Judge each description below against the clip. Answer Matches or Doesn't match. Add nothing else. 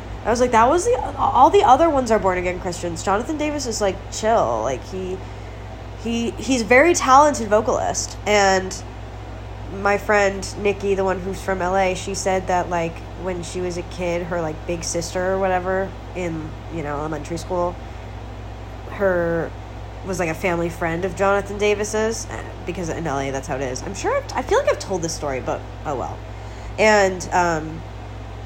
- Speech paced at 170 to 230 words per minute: Matches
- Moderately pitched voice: Matches